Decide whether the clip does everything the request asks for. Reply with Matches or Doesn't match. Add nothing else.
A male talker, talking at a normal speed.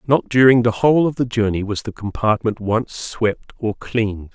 Matches